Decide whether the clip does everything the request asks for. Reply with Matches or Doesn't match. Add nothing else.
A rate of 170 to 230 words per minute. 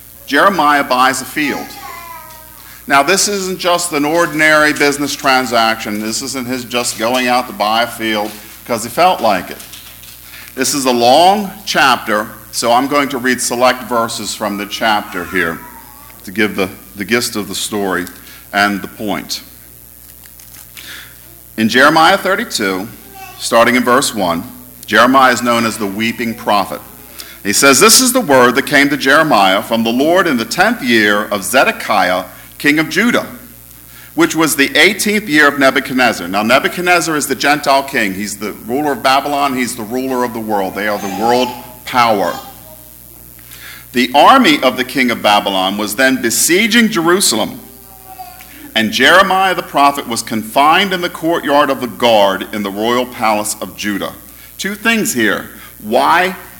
Doesn't match